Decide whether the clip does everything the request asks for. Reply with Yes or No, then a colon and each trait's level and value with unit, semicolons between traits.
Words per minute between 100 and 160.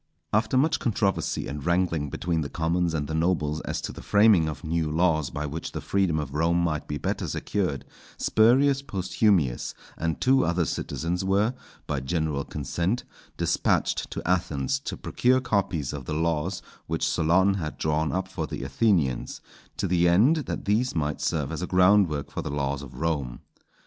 No: average, 175 wpm